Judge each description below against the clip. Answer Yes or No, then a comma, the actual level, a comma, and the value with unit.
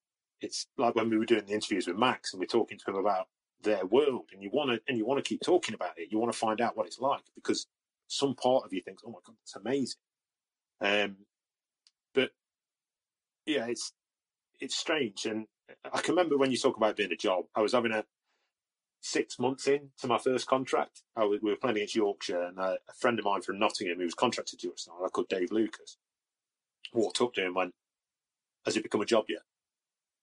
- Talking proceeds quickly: Yes, fast, 225 wpm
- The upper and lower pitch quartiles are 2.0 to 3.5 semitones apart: No, average, 4.2 semitones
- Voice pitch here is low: Yes, low, 115 Hz